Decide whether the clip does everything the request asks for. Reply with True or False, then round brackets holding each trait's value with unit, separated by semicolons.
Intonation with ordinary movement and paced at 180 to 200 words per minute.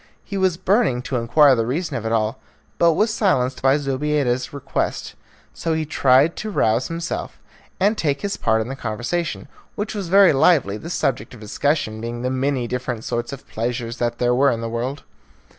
False (5.7 semitones; 195 wpm)